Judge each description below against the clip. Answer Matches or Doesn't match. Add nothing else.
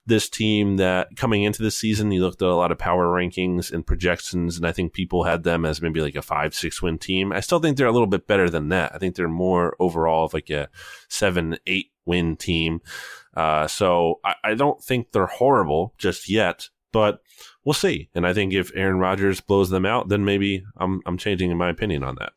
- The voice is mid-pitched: Doesn't match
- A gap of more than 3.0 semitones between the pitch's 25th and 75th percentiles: Doesn't match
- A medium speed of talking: Doesn't match